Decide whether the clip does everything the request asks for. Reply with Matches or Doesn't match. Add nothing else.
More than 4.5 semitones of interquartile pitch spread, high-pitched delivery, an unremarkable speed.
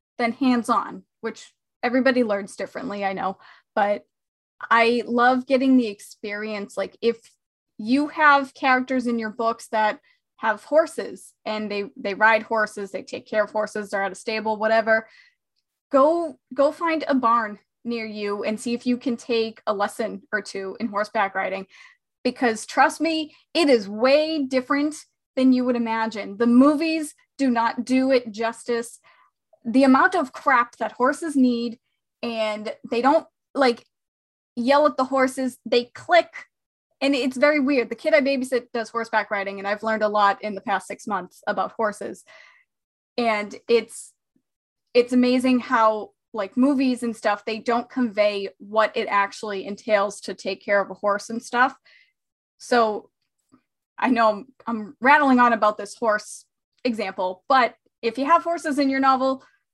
Doesn't match